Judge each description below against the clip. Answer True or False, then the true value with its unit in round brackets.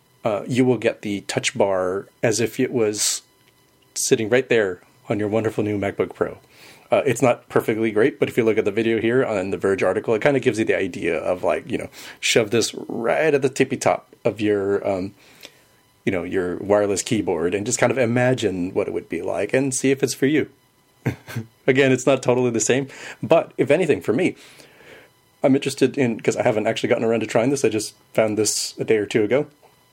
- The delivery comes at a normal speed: False (225 wpm)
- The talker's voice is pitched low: True (115 Hz)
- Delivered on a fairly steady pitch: False (3.7 semitones)